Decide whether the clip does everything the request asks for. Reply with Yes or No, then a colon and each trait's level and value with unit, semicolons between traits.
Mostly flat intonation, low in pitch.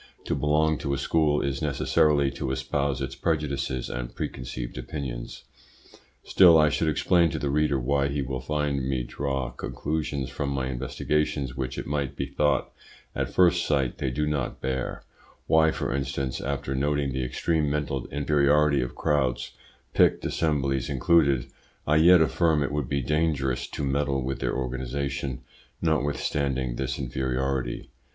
Yes: narrow, 2.2 semitones; very low, 70 Hz